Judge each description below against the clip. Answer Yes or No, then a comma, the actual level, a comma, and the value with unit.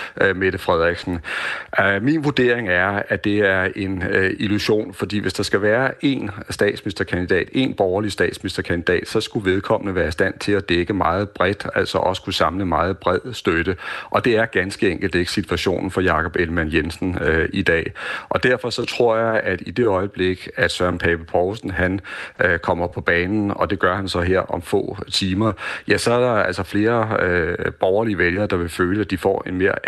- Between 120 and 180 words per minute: No, average, 195 wpm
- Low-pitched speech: Yes, very low, 95 Hz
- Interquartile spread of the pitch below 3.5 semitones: Yes, narrow, 2.4 semitones